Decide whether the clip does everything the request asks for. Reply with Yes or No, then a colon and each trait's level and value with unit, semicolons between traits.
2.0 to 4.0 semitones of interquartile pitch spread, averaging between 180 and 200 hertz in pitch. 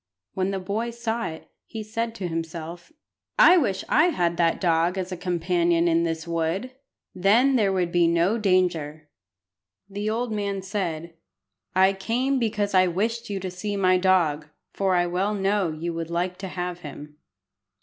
Yes: average, 3.5 semitones; medium, 185 Hz